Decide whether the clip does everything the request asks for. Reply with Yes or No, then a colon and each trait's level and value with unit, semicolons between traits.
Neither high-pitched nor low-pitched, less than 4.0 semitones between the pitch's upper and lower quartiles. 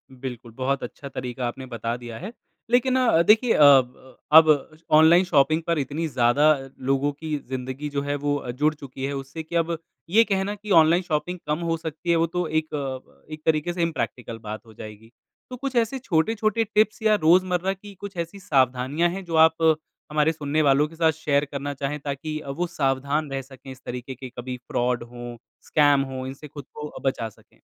No: medium, 150 Hz; average, 4.3 semitones